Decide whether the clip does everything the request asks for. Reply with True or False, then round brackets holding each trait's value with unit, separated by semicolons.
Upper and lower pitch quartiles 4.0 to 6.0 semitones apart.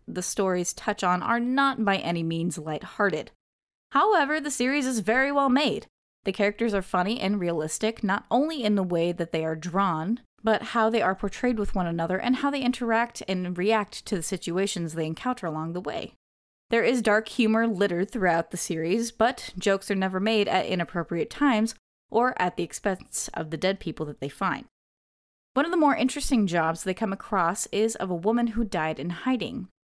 True (4.8 semitones)